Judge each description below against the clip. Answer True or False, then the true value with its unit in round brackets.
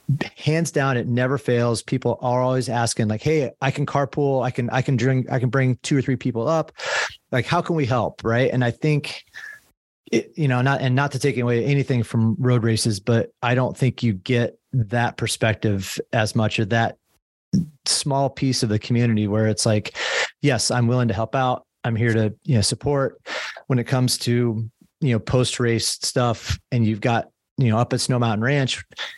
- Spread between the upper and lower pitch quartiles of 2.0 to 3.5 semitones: True (2.8 semitones)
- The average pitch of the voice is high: False (125 Hz)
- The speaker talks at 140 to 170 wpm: False (205 wpm)